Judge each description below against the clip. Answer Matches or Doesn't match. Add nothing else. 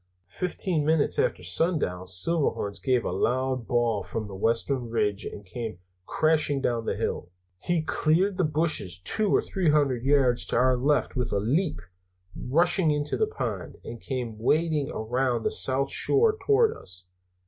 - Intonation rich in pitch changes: Matches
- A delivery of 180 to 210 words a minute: Doesn't match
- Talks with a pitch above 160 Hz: Doesn't match